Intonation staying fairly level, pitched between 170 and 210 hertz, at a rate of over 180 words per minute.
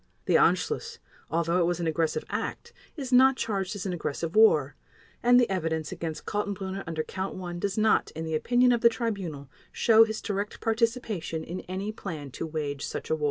No: wide, 5.4 semitones; high, 190 Hz; average, 195 wpm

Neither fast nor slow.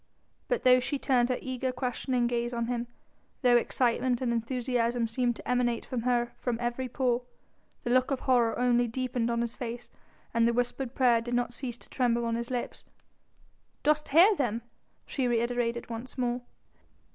Yes: average, 175 wpm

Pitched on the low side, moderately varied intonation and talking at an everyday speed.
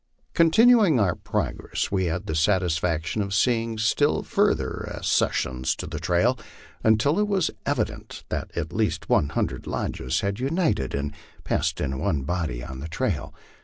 No: low, 100 Hz; wide, 7.9 semitones; average, 160 wpm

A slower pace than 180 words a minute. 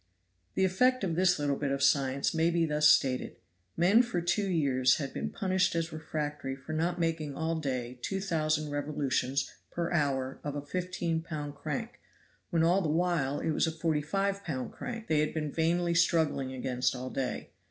No: average, 185 wpm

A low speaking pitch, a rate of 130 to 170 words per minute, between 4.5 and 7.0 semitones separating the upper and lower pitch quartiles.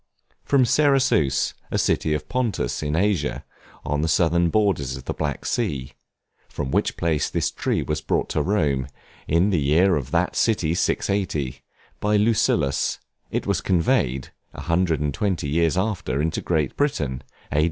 Yes: very low, 80 Hz; average, 165 wpm; wide, 5.4 semitones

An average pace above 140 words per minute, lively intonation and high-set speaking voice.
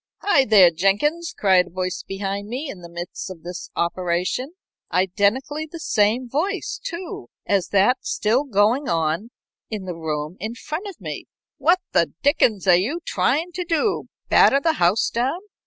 Yes: average, 165 wpm; wide, 8.3 semitones; high, 215 Hz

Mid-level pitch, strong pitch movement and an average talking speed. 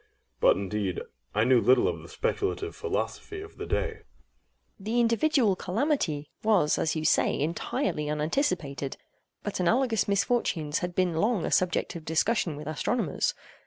Yes: medium, 180 Hz; wide, 7.7 semitones; average, 150 wpm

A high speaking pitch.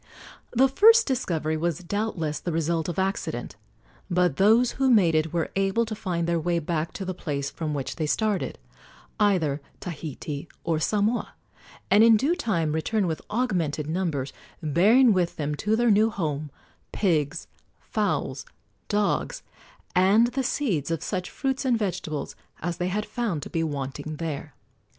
No: medium, 180 Hz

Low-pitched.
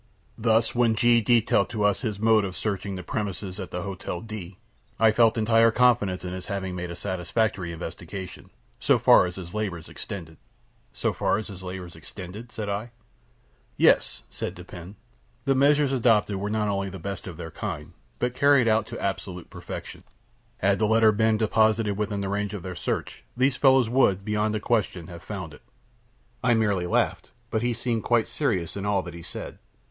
Yes: low, 105 Hz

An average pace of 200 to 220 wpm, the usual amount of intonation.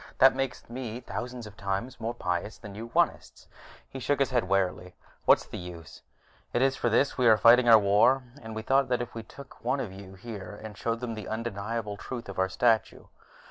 Yes: fast, 205 wpm; average, 3.8 semitones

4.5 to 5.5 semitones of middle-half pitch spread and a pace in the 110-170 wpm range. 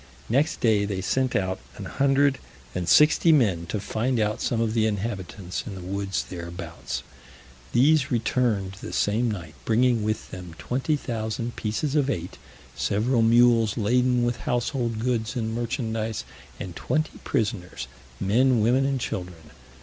No: average, 4.0 semitones; average, 145 wpm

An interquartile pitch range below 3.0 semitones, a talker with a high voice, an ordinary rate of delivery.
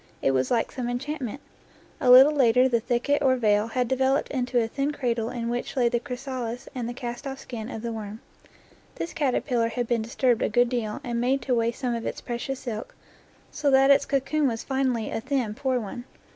No: narrow, 2.4 semitones; high, 245 Hz; fast, 215 wpm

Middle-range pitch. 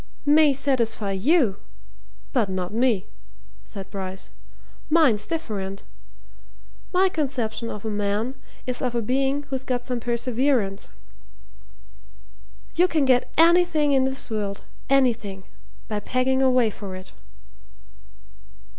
No: high, 245 Hz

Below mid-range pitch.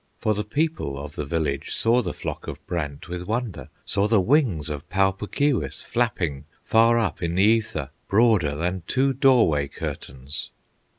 Yes: very low, 95 Hz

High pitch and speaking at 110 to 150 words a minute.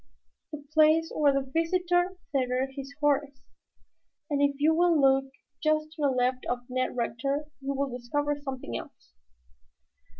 Yes: very high, 280 Hz; average, 145 wpm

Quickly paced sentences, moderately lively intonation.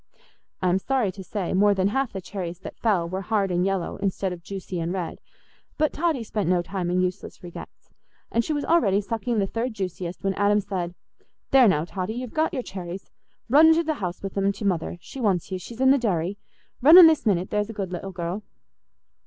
Yes: fast, 210 wpm; average, 4.0 semitones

